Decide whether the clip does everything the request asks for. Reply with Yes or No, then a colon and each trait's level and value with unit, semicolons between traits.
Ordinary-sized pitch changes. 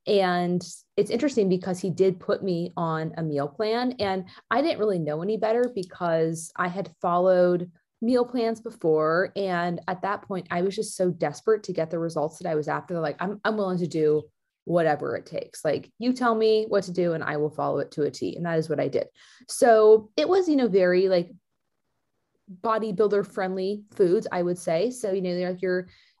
Yes: average, 4.1 semitones